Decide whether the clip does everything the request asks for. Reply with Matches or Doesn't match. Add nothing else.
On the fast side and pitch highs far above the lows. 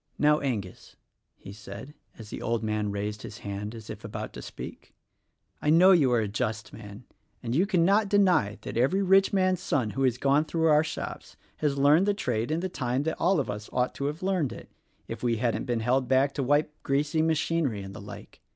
Matches